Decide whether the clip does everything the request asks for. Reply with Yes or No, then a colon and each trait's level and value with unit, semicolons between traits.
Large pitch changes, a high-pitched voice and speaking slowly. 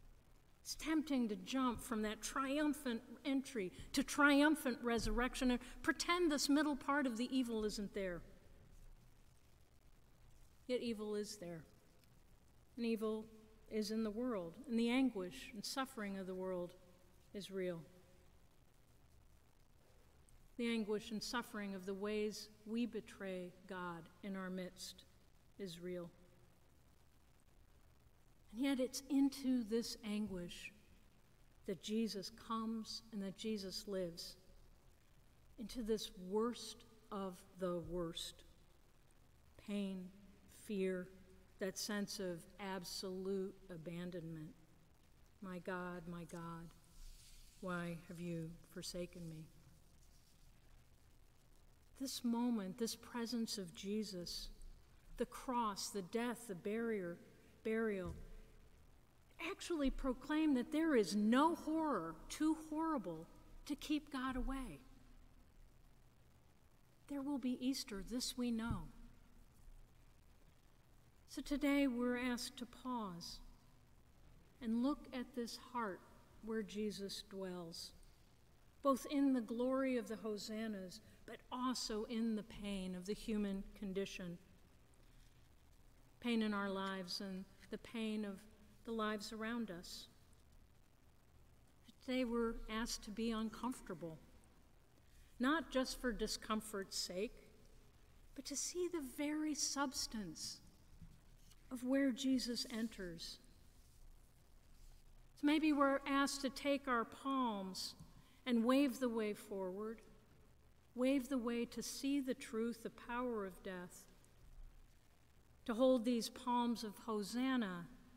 Yes: wide, 5.7 semitones; high, 215 Hz; slow, 110 wpm